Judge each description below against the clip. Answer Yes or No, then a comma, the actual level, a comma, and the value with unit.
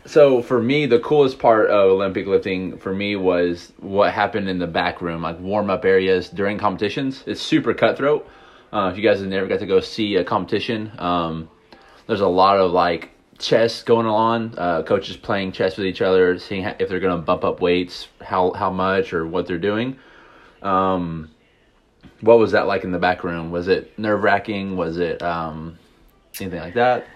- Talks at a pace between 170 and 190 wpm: No, average, 200 wpm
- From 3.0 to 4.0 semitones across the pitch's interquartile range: Yes, average, 3.6 semitones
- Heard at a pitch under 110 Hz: Yes, very low, 95 Hz